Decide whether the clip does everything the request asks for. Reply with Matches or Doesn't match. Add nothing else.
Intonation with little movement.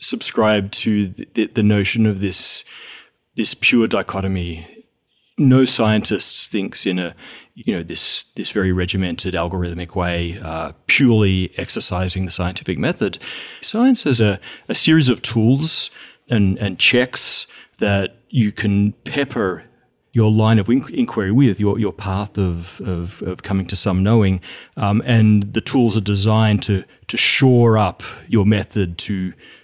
Doesn't match